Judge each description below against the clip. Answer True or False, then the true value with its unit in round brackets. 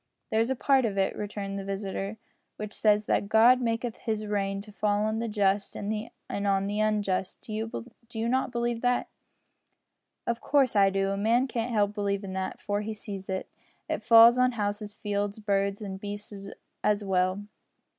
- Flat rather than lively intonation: True (2.3 semitones)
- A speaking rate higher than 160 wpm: True (175 wpm)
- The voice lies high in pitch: True (210 Hz)